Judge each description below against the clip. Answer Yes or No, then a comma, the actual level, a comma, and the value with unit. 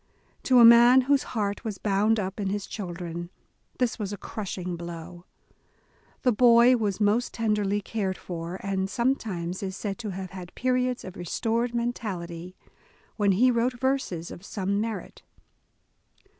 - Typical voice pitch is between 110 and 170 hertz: No, high, 205 Hz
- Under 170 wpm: Yes, average, 150 wpm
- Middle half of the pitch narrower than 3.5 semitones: No, average, 4.2 semitones